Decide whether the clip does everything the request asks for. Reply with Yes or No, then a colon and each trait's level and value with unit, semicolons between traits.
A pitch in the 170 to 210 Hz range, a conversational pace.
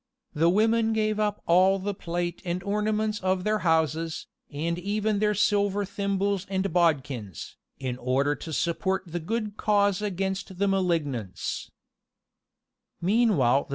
No: high, 190 Hz; slow, 125 wpm